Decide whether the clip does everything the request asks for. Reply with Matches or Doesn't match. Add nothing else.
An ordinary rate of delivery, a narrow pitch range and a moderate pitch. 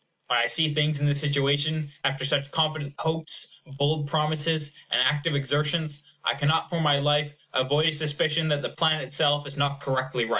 Matches